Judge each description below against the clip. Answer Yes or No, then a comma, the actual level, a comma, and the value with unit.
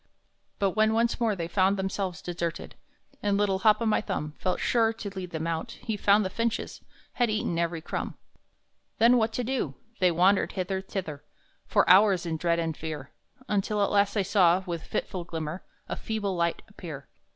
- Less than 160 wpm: No, average, 185 wpm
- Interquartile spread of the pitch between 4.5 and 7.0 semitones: No, average, 3.9 semitones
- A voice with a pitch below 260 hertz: Yes, high, 190 Hz